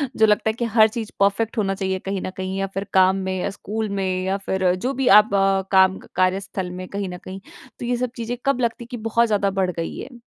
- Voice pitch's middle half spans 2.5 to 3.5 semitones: Yes, average, 3.1 semitones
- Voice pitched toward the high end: Yes, high, 195 Hz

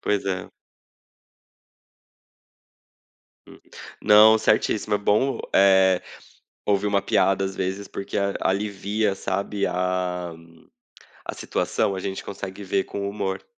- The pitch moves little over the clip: Yes, narrow, 1.3 semitones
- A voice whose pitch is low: Yes, low, 100 Hz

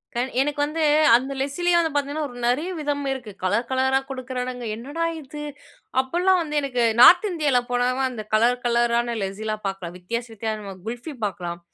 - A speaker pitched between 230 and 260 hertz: Yes, very high, 250 Hz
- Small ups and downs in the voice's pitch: No, average, 4.0 semitones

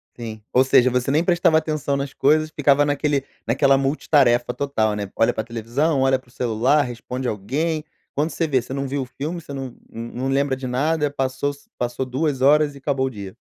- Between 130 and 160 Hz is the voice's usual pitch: Yes, low, 135 Hz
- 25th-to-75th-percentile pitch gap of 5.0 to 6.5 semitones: No, average, 2.9 semitones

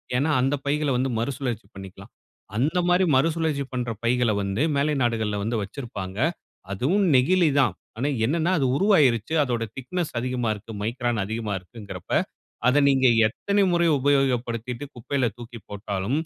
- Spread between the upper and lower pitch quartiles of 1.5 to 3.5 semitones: No, average, 4.2 semitones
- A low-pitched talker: Yes, low, 125 Hz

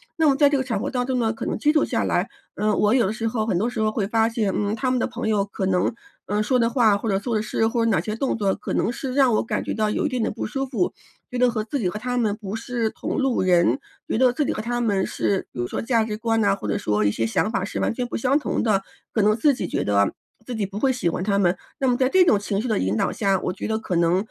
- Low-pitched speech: No, high, 220 Hz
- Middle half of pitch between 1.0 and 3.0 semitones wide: No, average, 3.7 semitones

